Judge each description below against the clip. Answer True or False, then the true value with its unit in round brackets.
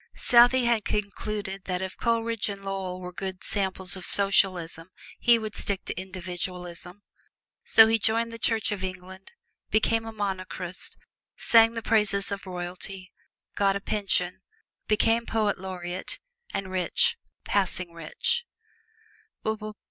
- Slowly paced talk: True (130 wpm)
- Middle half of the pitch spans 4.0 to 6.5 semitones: False (3.1 semitones)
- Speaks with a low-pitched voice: False (195 Hz)